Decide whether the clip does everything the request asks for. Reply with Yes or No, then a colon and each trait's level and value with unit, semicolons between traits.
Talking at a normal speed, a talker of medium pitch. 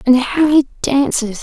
No: average, 170 wpm; very high, 265 Hz